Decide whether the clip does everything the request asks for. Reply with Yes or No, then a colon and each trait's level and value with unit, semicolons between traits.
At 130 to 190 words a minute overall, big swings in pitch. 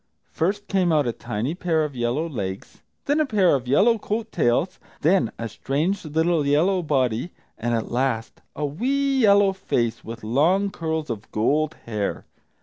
Yes: average, 160 wpm; wide, 8.1 semitones